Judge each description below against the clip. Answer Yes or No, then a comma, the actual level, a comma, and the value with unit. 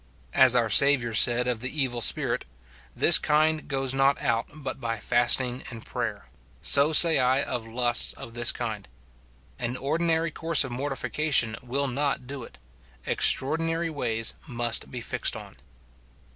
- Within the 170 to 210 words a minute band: No, average, 160 wpm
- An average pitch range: Yes, average, 3.3 semitones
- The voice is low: Yes, low, 130 Hz